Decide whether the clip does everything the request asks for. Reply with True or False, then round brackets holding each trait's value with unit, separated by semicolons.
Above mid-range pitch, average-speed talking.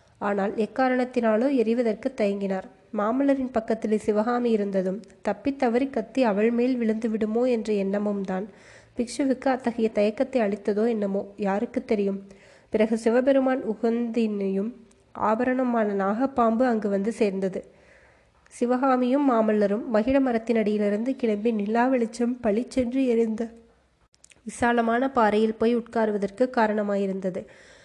True (225 Hz; 100 wpm)